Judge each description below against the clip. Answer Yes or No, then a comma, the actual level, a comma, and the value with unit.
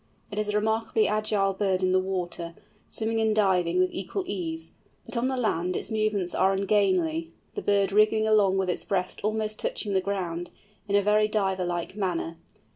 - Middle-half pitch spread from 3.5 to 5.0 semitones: No, average, 2.8 semitones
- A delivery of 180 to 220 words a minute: Yes, average, 190 wpm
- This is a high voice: Yes, high, 195 Hz